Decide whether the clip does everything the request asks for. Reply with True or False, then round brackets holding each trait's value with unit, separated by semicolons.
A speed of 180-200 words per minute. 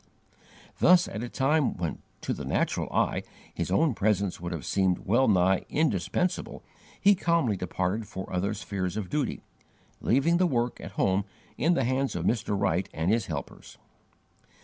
False (165 wpm)